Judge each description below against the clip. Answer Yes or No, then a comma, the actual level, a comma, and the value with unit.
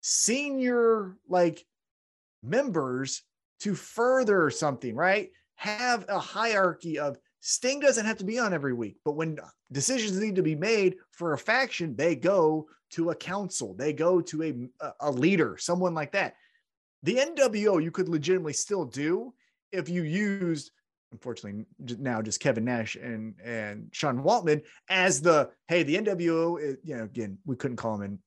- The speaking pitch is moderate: Yes, medium, 170 Hz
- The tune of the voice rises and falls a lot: Yes, wide, 7.0 semitones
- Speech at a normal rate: Yes, average, 160 wpm